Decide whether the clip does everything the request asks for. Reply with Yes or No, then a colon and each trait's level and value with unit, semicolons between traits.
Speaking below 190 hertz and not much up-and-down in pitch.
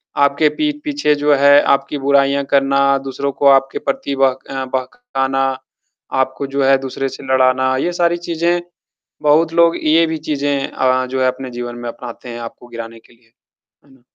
Yes: low, 135 Hz; narrow, 2.2 semitones